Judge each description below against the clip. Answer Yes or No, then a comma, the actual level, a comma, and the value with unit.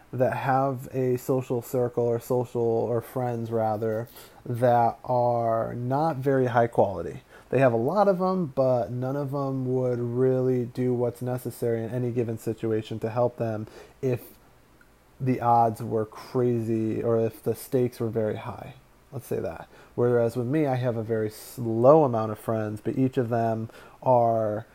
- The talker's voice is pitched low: Yes, low, 120 Hz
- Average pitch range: No, narrow, 2.0 semitones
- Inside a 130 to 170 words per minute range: Yes, average, 165 wpm